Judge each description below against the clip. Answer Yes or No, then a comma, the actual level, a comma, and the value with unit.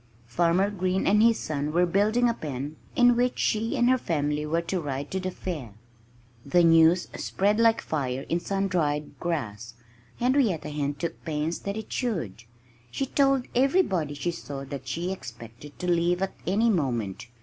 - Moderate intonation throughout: No, wide, 5.9 semitones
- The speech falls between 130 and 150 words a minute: No, average, 170 wpm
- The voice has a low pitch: No, medium, 170 Hz